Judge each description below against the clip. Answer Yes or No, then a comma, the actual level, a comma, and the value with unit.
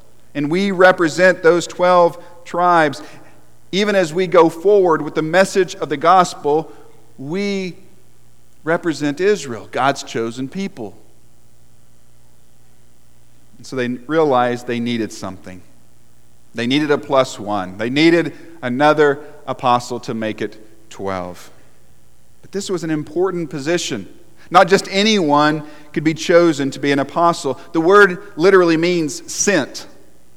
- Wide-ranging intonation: Yes, wide, 7.3 semitones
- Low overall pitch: No, medium, 150 Hz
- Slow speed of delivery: Yes, slow, 125 wpm